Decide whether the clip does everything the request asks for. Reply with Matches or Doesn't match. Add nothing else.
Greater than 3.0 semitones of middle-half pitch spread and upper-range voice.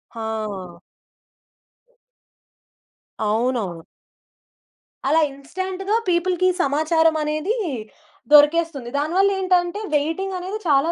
Matches